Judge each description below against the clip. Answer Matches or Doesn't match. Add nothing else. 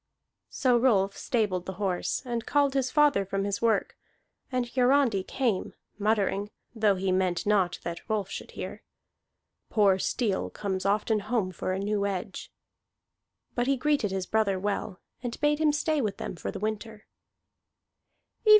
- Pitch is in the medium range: Doesn't match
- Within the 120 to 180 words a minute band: Matches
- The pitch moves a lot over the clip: Doesn't match